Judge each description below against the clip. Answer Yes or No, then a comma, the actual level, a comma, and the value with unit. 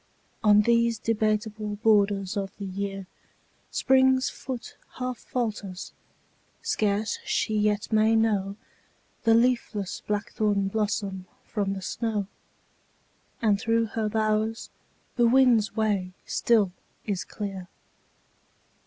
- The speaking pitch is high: Yes, high, 215 Hz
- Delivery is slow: Yes, slow, 105 wpm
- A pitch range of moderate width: No, narrow, 2.1 semitones